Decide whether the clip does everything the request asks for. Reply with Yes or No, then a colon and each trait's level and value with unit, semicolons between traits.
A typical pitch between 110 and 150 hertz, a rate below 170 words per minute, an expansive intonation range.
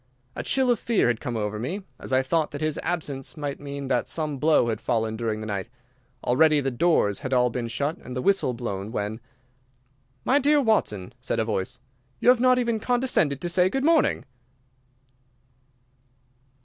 No: medium, 140 Hz; average, 185 wpm; wide, 8.2 semitones